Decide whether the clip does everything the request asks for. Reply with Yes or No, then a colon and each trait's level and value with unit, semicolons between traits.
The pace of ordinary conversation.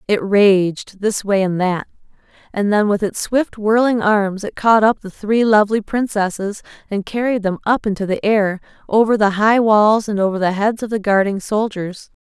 Yes: average, 190 wpm